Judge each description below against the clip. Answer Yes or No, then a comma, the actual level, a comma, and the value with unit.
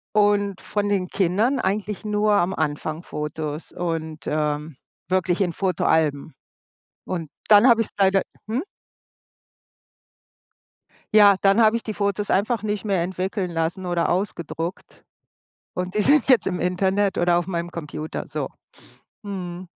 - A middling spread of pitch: Yes, average, 3.4 semitones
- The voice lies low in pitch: No, medium, 185 Hz